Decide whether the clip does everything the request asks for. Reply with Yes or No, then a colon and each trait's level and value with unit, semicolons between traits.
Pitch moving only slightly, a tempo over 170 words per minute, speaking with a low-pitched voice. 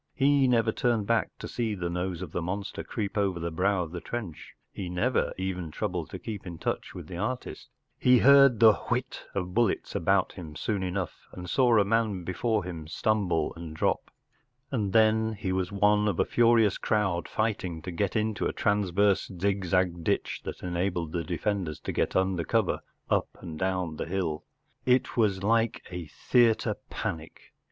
No: average, 3.8 semitones; average, 180 wpm; very low, 95 Hz